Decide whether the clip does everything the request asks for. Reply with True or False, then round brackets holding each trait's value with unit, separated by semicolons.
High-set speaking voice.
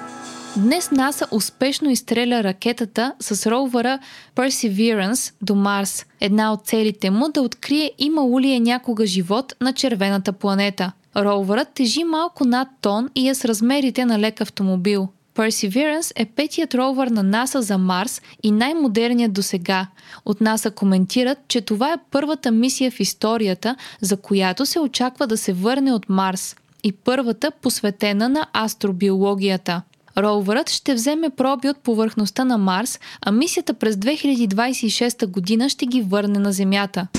True (230 Hz)